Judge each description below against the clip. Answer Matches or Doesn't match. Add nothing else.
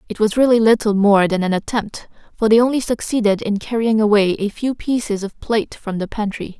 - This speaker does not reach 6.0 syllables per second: Matches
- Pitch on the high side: Matches